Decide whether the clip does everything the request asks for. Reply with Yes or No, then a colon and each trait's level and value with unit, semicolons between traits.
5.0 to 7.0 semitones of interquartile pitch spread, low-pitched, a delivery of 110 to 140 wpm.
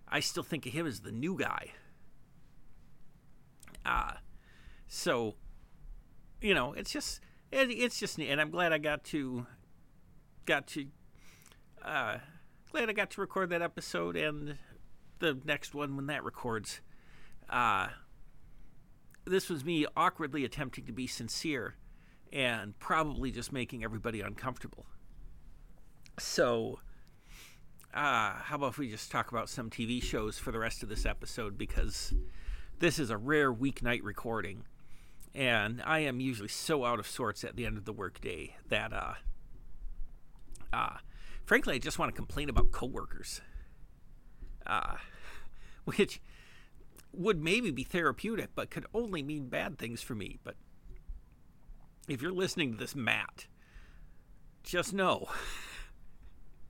Yes: wide, 5.5 semitones; low, 130 Hz; slow, 135 wpm